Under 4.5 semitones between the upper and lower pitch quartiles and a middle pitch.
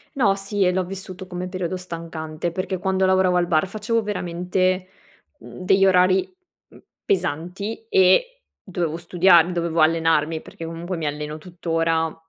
Yes: narrow, 2.5 semitones; medium, 180 Hz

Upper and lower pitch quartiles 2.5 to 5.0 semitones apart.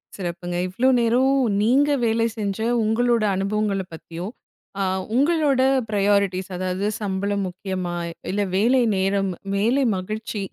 Yes: average, 3.7 semitones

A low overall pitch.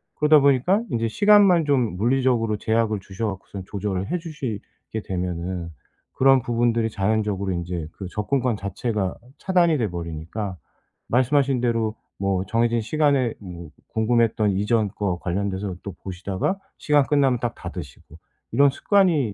Yes: low, 110 Hz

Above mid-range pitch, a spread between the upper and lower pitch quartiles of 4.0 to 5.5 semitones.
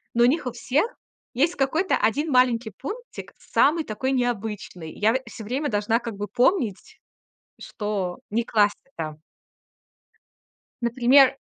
Yes: high, 240 Hz; average, 4.4 semitones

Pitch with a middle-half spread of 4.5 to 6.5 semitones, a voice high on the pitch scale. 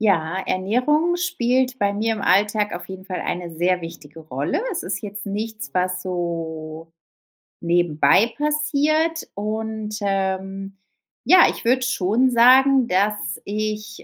Yes: average, 5.3 semitones; high, 205 Hz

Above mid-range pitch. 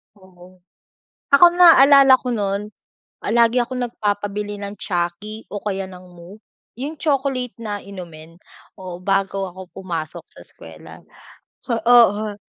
Yes: high, 205 Hz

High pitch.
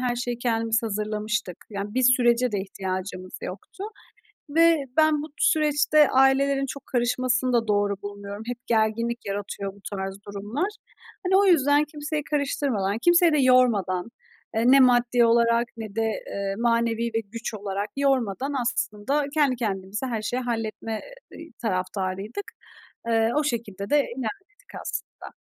Yes: high, 235 Hz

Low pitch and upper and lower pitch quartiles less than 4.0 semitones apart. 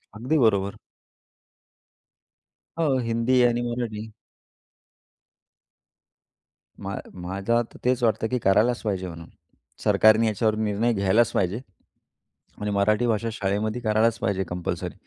Yes: low, 110 Hz; average, 2.9 semitones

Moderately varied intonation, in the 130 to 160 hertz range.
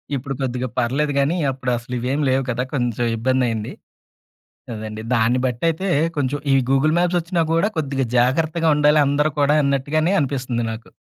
Yes: average, 3.3 semitones; low, 135 Hz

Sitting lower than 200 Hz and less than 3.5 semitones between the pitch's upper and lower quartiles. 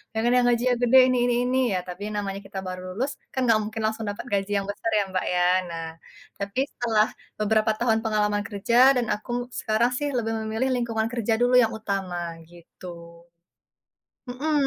No: high, 220 Hz; average, 3.0 semitones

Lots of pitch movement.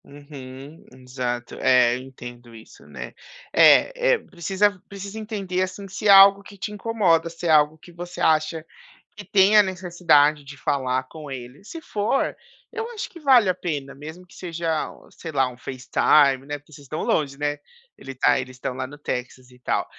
Yes: wide, 6.3 semitones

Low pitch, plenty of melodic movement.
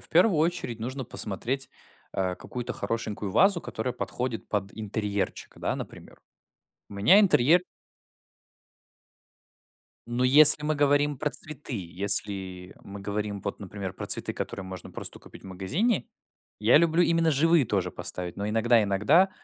Yes: low, 115 Hz; wide, 7.0 semitones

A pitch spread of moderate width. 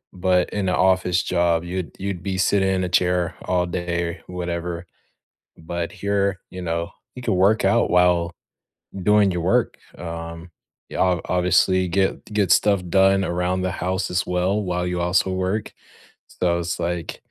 No: narrow, 1.5 semitones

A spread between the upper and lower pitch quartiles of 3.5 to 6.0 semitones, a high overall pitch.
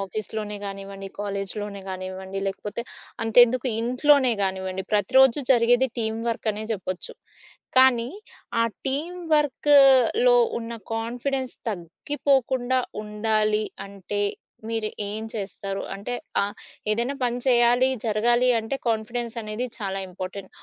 Yes: average, 4.0 semitones; high, 225 Hz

